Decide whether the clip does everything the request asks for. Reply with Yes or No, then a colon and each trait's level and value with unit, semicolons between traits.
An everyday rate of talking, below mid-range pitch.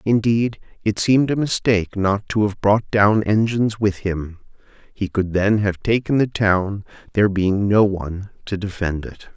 Yes: average, 175 wpm; low, 105 Hz